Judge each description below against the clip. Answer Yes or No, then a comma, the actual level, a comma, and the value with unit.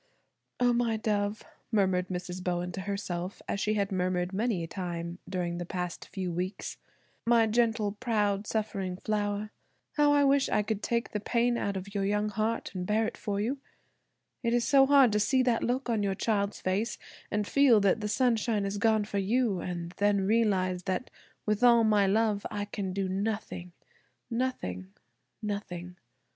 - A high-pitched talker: Yes, high, 205 Hz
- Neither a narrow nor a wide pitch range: Yes, average, 3.4 semitones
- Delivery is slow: No, average, 175 wpm